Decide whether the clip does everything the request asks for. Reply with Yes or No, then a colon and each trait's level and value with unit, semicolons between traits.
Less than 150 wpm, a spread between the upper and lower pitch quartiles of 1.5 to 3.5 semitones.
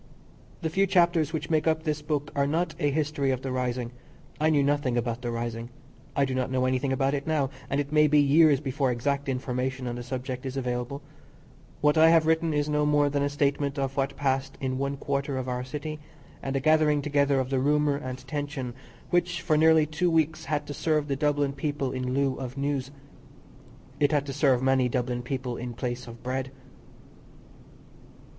No: fast, 205 wpm; narrow, 2.5 semitones